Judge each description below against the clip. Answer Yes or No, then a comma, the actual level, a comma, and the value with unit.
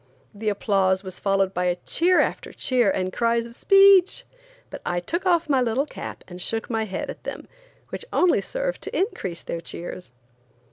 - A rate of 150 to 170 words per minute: No, average, 180 wpm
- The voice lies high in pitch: Yes, high, 225 Hz